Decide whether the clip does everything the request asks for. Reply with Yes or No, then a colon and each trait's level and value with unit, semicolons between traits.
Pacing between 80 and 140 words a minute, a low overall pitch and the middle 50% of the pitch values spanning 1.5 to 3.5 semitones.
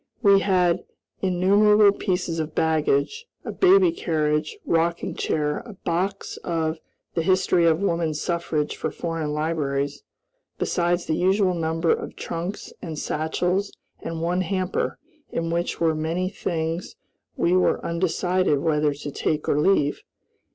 No: slow, 135 wpm; medium, 170 Hz; average, 2.7 semitones